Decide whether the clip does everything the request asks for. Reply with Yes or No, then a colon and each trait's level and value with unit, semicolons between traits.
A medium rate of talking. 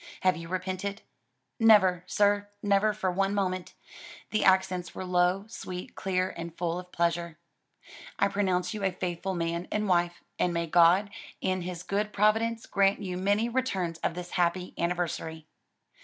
Yes: average, 155 wpm